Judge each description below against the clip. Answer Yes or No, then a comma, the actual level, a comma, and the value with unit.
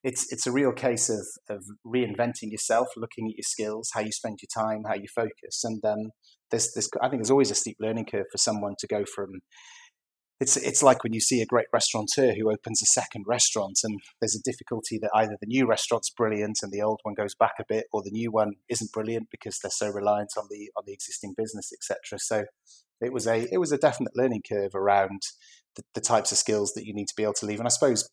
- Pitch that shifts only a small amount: Yes, narrow, 2.0 semitones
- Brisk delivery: Yes, fast, 245 wpm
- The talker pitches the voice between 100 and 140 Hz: Yes, low, 110 Hz